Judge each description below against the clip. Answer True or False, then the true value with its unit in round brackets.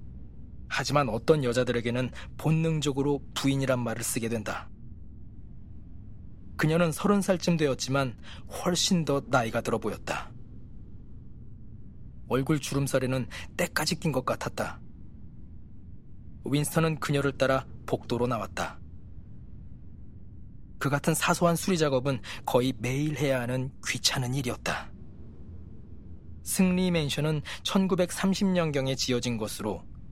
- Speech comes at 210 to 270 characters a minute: True (235 characters per minute)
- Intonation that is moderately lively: False (5.7 semitones)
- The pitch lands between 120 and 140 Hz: True (130 Hz)